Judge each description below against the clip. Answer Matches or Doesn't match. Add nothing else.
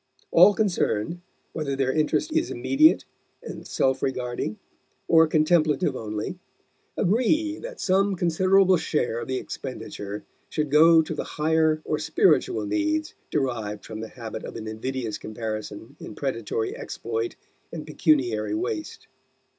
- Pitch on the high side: Doesn't match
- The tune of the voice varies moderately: Doesn't match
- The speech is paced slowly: Matches